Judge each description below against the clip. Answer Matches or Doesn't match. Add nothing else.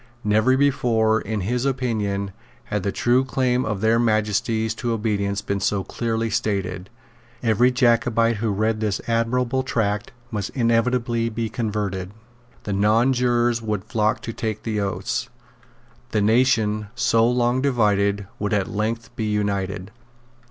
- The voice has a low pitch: Matches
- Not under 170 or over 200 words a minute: Doesn't match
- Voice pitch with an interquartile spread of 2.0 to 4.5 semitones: Matches